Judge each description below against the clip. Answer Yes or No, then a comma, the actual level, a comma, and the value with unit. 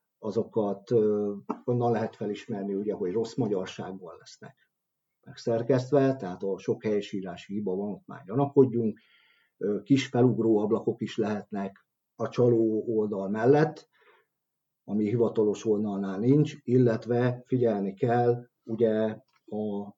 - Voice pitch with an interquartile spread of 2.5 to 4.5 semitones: Yes, average, 2.9 semitones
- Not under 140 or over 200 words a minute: No, average, 110 wpm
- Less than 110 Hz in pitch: No, low, 115 Hz